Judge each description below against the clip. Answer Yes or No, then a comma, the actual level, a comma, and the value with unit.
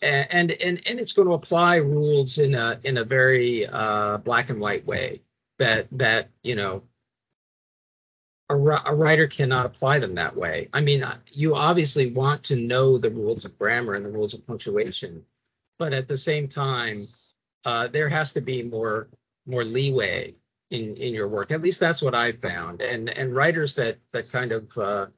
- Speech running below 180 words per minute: No, average, 185 wpm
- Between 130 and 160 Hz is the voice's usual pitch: Yes, low, 135 Hz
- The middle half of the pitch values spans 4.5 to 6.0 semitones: No, average, 4.0 semitones